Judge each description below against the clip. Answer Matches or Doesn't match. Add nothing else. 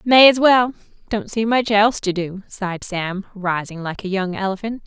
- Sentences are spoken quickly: Doesn't match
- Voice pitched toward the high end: Matches